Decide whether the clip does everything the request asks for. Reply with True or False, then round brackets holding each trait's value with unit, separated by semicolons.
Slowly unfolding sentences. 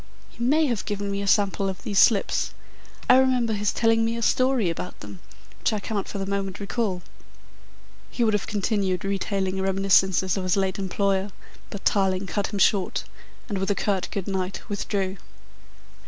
False (180 wpm)